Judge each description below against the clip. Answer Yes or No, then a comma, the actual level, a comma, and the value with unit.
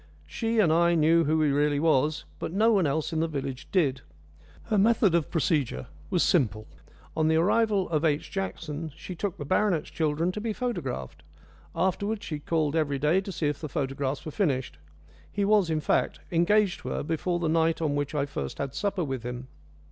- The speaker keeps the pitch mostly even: No, average, 4.3 semitones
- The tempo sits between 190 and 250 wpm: Yes, average, 200 wpm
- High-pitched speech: No, medium, 160 Hz